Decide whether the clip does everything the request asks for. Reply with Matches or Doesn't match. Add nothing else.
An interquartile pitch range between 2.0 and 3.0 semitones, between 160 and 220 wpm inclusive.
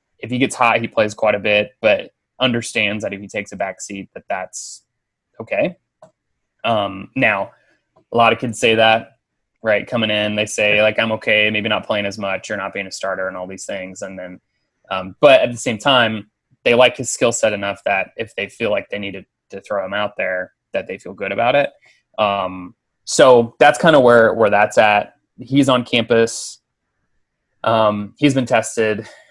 Matches